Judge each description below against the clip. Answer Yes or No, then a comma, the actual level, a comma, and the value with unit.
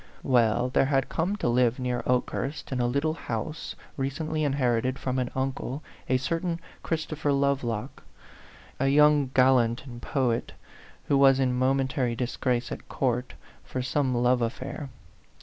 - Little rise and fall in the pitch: Yes, narrow, 2.3 semitones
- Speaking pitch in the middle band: No, low, 130 Hz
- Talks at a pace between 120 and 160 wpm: Yes, average, 150 wpm